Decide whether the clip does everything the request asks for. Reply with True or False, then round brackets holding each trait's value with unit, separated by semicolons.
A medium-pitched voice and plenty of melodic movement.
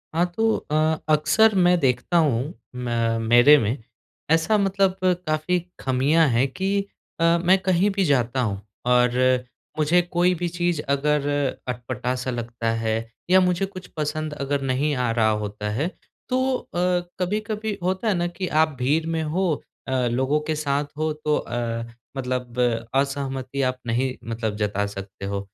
True (145 Hz; 6.0 semitones)